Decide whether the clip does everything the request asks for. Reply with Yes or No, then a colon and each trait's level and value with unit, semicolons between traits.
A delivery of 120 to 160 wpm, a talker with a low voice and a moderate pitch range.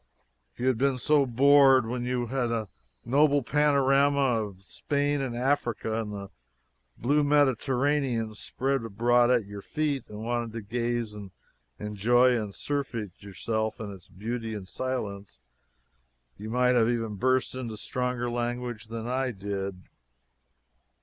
Yes: average, 145 wpm; low, 120 Hz; average, 3.2 semitones